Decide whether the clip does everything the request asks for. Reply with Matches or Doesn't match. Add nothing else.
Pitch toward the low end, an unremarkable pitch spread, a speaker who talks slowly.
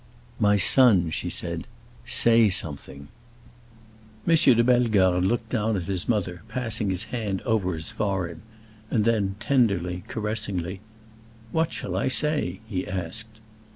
Matches